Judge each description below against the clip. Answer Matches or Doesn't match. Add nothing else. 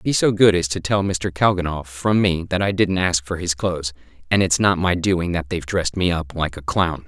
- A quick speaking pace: Matches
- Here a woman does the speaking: Doesn't match